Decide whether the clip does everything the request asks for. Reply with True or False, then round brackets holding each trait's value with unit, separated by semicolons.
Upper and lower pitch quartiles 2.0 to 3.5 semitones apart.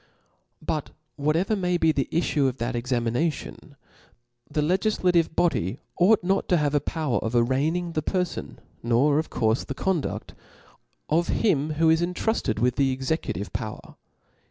False (5.1 semitones)